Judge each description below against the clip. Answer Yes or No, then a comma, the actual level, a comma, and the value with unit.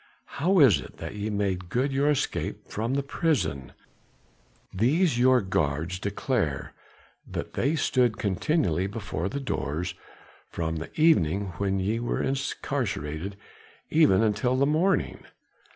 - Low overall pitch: Yes, low, 105 Hz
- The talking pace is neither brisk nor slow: No, slow, 130 wpm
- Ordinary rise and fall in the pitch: No, wide, 7.0 semitones